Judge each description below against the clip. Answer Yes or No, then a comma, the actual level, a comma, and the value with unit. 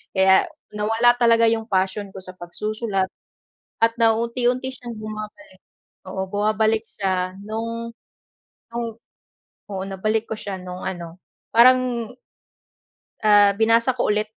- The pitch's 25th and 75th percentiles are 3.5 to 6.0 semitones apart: No, average, 3.0 semitones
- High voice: Yes, high, 215 Hz